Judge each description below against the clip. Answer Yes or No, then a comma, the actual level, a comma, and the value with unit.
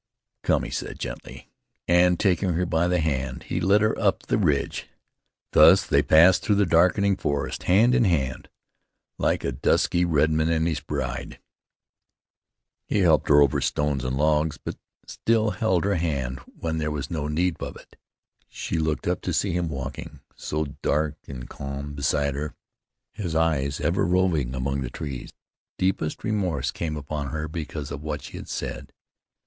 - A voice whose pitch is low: Yes, very low, 80 Hz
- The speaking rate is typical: Yes, average, 170 wpm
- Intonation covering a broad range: No, average, 3.9 semitones